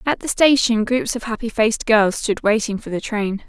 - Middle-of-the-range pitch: No, high, 225 Hz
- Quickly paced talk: Yes, fast, 225 wpm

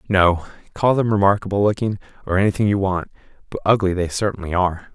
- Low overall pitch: Yes, low, 100 Hz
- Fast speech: No, average, 160 wpm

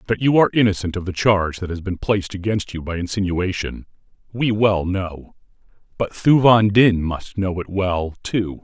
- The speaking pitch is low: Yes, very low, 95 Hz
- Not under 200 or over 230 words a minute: No, average, 180 wpm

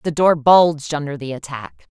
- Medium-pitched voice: Yes, medium, 150 Hz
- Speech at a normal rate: Yes, average, 185 wpm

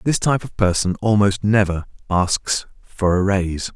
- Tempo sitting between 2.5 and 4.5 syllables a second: No, 4.9 syllables/s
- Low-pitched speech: Yes, low, 100 Hz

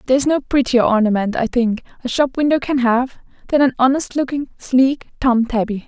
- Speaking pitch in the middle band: No, very high, 255 Hz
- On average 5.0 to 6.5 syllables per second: Yes, 5.4 syllables/s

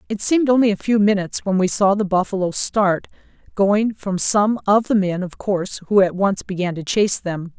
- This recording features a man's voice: No, female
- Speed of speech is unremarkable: No, fast, 215 wpm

